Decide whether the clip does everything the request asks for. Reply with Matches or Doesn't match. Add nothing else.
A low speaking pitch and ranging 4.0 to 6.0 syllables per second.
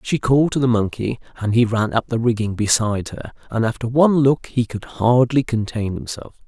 Matches